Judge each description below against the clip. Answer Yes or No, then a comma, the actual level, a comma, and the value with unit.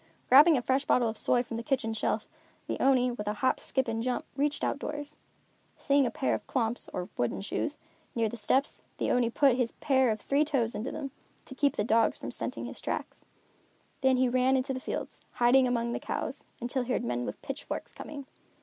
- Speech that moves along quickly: Yes, fast, 215 wpm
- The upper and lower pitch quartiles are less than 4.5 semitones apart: Yes, average, 2.9 semitones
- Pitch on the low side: No, very high, 255 Hz